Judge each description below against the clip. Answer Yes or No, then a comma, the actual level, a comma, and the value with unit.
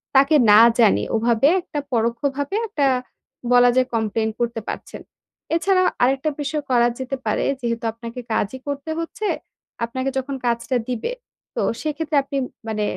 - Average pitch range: Yes, average, 3.6 semitones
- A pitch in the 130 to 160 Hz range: No, very high, 255 Hz